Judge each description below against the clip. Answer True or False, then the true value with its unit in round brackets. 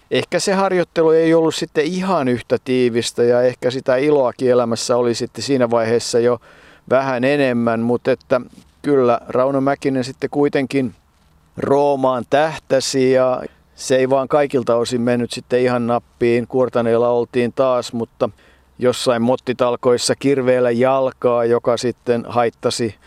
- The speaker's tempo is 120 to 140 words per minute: True (135 wpm)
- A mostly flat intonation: True (2.3 semitones)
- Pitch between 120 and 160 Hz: True (125 Hz)